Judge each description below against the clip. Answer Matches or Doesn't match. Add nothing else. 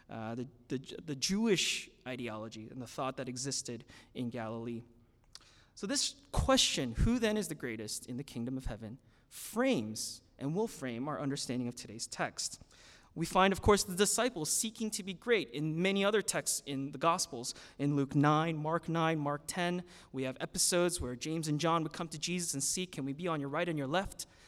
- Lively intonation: Matches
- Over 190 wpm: Matches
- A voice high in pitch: Doesn't match